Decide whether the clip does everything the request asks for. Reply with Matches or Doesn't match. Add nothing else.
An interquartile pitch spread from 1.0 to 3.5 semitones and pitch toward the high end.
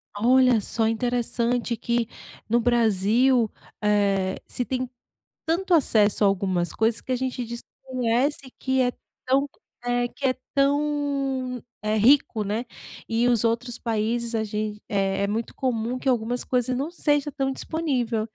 Matches